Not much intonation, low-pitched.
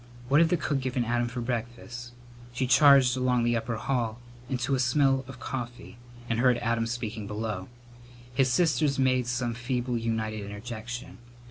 Yes: narrow, 2.0 semitones; low, 120 Hz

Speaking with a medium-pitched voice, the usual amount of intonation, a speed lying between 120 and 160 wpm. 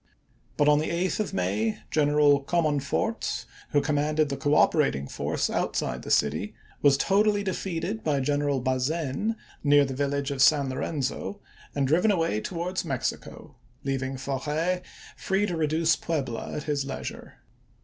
Yes: medium, 145 Hz; average, 3.5 semitones; average, 150 wpm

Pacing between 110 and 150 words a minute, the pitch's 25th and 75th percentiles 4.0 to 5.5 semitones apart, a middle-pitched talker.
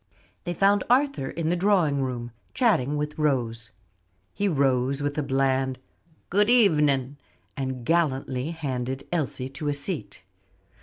Yes: slow, 135 wpm; average, 4.5 semitones; medium, 145 Hz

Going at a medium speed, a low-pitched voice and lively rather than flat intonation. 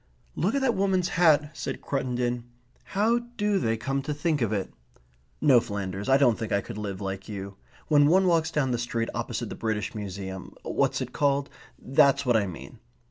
Yes: average, 190 wpm; low, 130 Hz; wide, 6.7 semitones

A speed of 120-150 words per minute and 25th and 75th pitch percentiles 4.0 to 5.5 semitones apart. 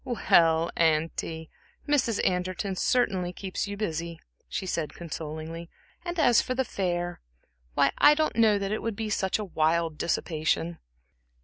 Yes: average, 140 wpm; average, 4.7 semitones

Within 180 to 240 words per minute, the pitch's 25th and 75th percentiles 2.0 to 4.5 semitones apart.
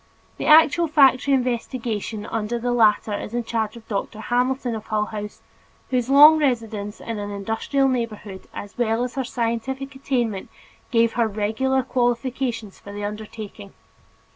No: average, 150 wpm; average, 3.4 semitones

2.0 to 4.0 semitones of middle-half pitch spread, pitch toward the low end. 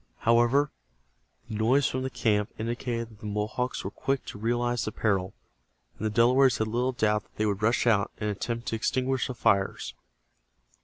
Yes: average, 2.7 semitones; low, 115 Hz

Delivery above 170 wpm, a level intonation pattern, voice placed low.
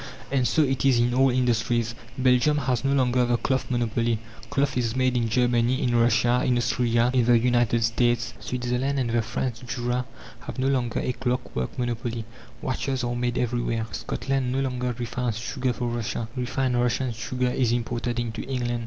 Yes: average, 180 wpm; narrow, 1.3 semitones; low, 120 Hz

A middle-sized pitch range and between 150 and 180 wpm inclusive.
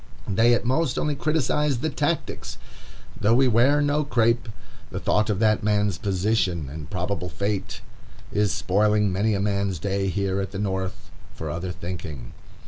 Yes: average, 3.9 semitones; average, 160 wpm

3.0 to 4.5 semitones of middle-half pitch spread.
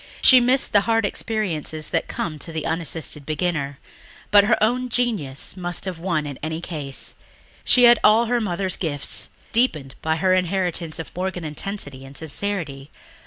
No: average, 5.2 semitones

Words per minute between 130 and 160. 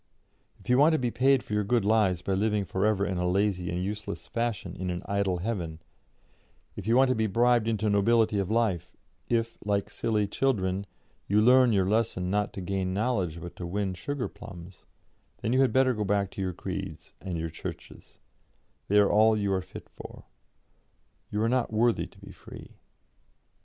No: average, 195 wpm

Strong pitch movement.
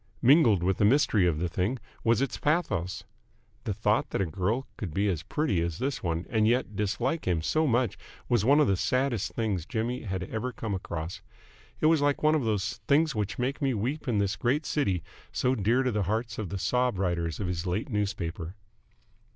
Yes: wide, 5.8 semitones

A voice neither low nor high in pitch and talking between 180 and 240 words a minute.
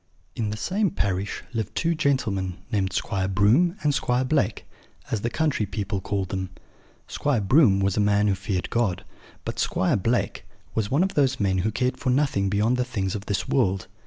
No: low, 105 Hz; average, 190 wpm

